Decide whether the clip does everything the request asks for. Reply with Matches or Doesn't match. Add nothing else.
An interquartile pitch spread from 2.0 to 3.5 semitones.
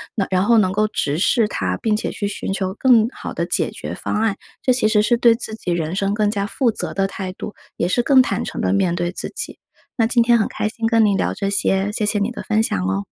Matches